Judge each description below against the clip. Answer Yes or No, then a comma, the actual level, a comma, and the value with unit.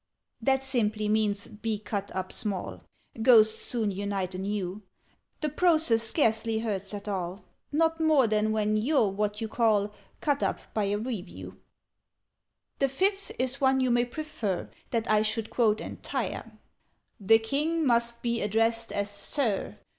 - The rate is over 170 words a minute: No, average, 145 wpm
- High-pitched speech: Yes, high, 220 Hz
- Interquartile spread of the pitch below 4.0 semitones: Yes, average, 3.6 semitones